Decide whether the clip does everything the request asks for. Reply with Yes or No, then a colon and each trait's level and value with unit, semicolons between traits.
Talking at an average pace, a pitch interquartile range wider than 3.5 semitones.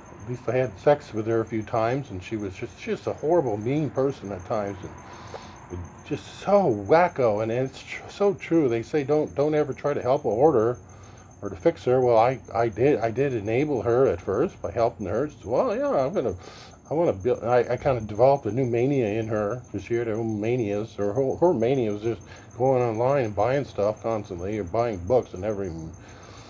No: fast, 220 wpm; average, 4.1 semitones